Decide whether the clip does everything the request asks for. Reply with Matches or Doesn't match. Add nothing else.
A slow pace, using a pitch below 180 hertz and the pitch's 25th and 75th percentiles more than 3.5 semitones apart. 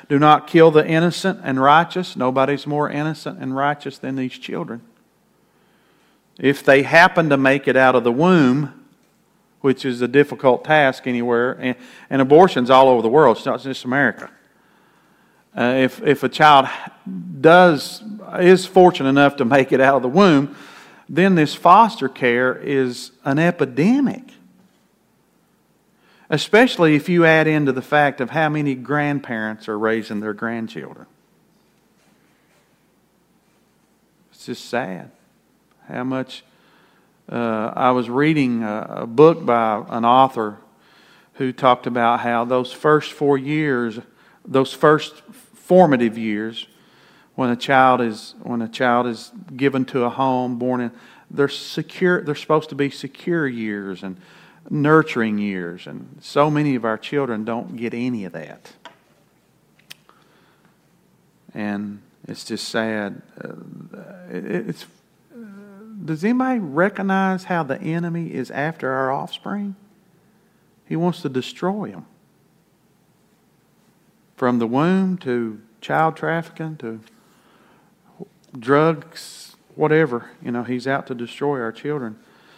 Matches